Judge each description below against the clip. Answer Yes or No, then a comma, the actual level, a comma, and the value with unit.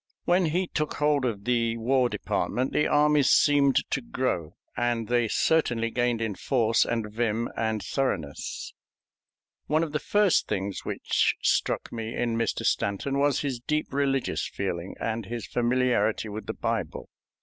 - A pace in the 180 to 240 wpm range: No, average, 155 wpm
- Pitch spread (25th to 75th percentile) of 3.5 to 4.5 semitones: Yes, average, 3.9 semitones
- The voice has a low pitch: Yes, low, 120 Hz